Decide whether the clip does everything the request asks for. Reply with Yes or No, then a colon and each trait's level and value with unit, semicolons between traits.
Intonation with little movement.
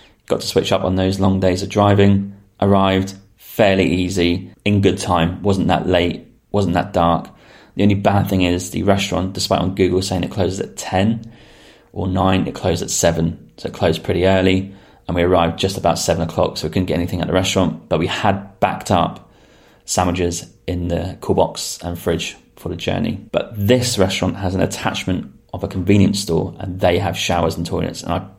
Yes: narrow, 2.0 semitones